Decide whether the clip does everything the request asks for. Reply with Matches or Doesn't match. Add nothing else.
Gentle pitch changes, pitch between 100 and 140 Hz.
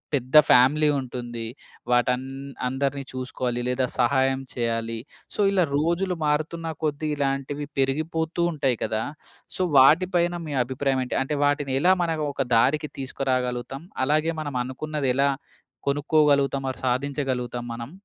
Doesn't match